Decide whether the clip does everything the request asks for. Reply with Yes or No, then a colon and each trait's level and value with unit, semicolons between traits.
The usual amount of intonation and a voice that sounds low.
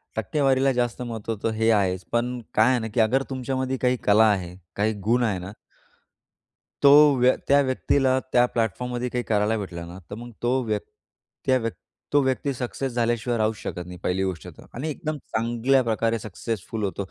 Yes: average, 3.3 semitones; low, 115 Hz